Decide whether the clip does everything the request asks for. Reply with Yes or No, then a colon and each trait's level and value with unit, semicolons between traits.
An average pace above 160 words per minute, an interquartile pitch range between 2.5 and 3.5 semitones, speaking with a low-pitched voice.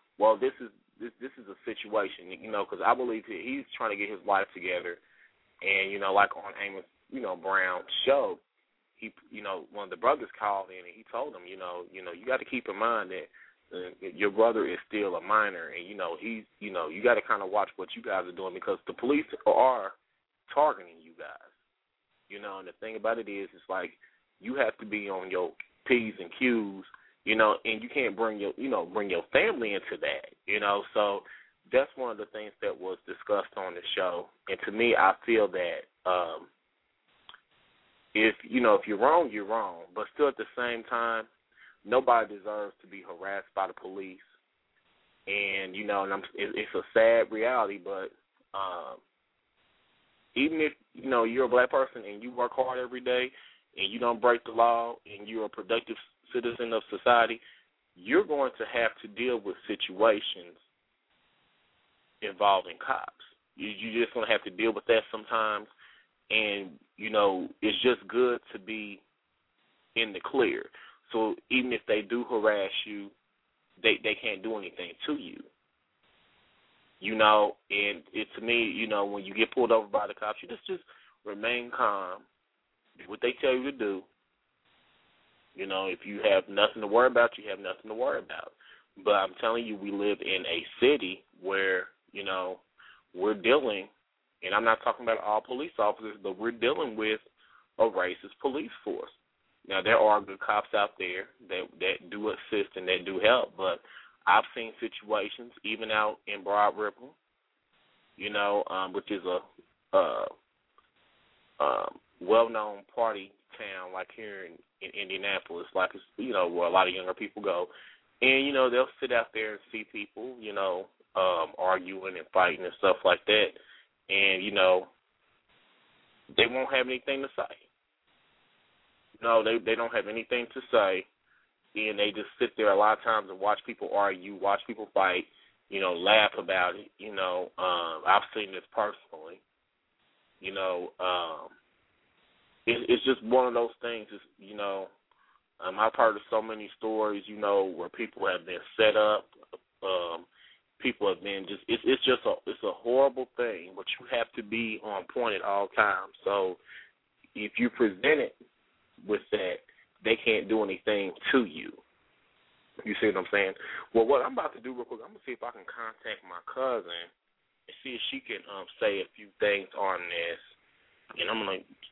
No: average, 185 wpm; average, 4.3 semitones; low, 110 Hz